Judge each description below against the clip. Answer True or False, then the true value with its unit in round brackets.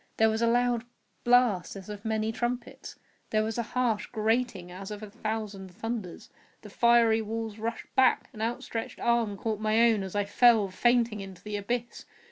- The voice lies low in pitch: False (220 Hz)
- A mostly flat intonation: True (2.3 semitones)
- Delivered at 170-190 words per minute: True (180 wpm)